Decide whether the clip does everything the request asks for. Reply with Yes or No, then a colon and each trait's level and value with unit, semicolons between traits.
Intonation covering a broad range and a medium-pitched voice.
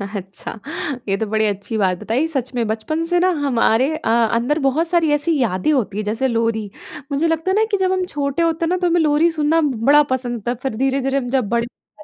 No: wide, 6.2 semitones; very high, 265 Hz